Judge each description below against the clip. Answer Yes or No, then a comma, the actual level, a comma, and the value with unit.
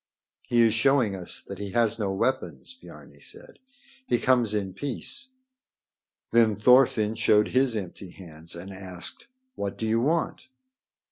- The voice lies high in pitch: No, low, 110 Hz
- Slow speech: No, average, 145 wpm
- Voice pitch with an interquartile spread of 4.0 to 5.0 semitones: Yes, average, 4.6 semitones